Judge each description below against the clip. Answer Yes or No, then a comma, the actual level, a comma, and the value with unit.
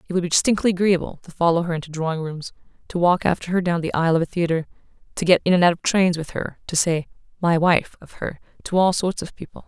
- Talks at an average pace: No, fast, 255 wpm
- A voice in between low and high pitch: Yes, medium, 170 Hz